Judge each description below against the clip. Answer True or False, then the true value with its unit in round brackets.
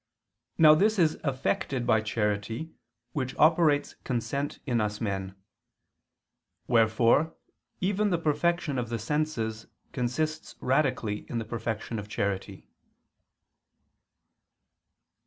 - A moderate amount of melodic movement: False (5.8 semitones)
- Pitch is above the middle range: False (125 Hz)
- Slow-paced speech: True (100 wpm)